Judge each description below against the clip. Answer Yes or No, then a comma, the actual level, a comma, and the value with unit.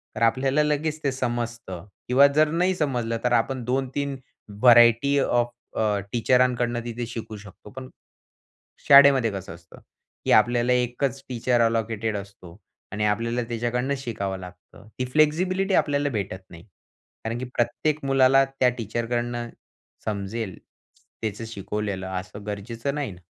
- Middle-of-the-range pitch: No, low, 120 Hz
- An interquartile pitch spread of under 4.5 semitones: Yes, average, 3.8 semitones